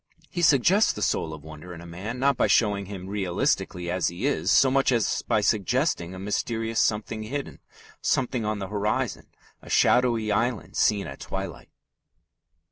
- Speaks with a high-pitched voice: No, low, 105 Hz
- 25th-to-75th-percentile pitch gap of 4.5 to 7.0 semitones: Yes, average, 4.8 semitones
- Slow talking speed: No, average, 170 wpm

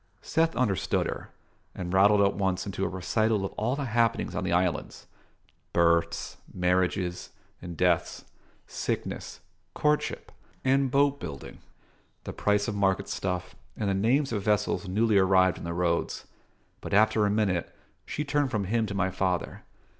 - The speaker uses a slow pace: No, average, 155 wpm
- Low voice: Yes, low, 100 Hz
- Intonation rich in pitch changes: No, average, 3.5 semitones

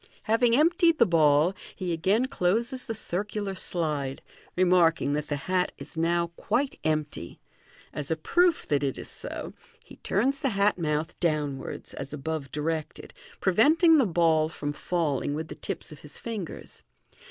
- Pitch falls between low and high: Yes, medium, 170 Hz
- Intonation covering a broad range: Yes, wide, 6.3 semitones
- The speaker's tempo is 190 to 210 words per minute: No, average, 155 wpm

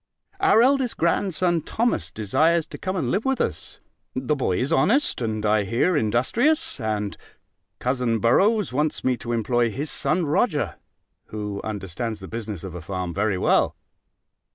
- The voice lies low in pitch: Yes, low, 125 Hz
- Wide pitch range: Yes, wide, 8.5 semitones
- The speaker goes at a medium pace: Yes, average, 155 wpm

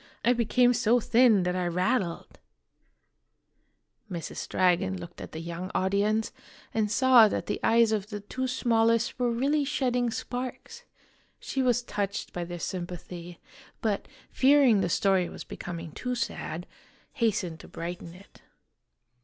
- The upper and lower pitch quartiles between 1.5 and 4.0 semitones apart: No, wide, 5.5 semitones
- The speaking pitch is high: Yes, high, 210 Hz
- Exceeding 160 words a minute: No, average, 145 wpm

